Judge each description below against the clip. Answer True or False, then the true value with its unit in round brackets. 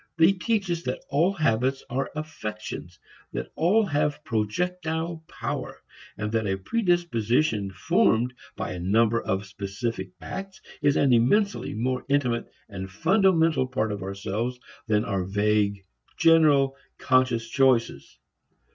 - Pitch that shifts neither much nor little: False (7.2 semitones)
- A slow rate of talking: True (130 wpm)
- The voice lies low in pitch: True (125 Hz)